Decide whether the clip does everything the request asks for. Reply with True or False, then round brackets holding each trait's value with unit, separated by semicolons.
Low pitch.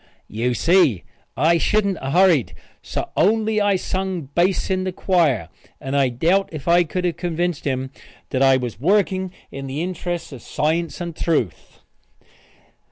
False (170 Hz)